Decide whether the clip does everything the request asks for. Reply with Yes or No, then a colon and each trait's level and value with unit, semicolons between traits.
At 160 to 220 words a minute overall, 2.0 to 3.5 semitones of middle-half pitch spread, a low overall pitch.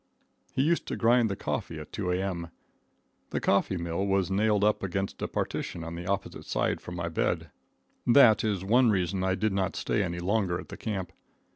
Yes: average, 195 wpm; average, 3.2 semitones; very low, 95 Hz